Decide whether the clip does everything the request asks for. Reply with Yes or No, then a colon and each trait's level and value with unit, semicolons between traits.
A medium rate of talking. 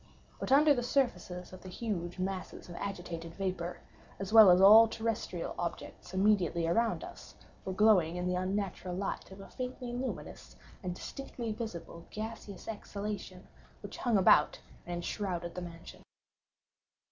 Yes: average, 145 wpm